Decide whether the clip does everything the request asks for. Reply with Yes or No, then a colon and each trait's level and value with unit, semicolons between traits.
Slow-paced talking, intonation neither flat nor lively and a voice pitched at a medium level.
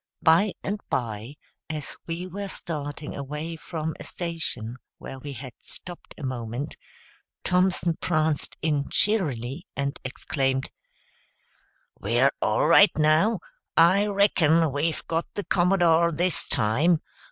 Yes: slow, 120 wpm; average, 4.1 semitones; medium, 155 Hz